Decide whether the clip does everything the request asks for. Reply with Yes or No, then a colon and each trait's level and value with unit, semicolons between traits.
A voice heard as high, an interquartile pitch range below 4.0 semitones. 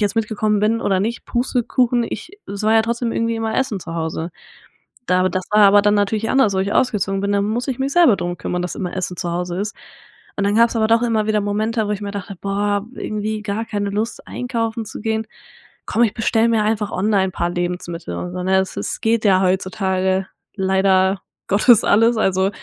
Yes: high, 205 Hz; average, 2.9 semitones